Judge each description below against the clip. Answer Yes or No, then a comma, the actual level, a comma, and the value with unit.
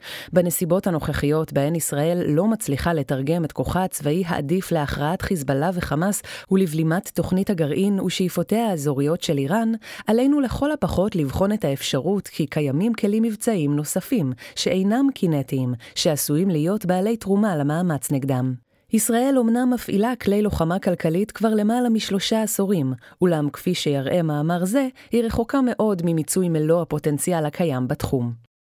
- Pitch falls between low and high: Yes, medium, 175 Hz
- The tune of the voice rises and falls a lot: Yes, wide, 5.9 semitones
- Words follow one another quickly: No, average, 130 wpm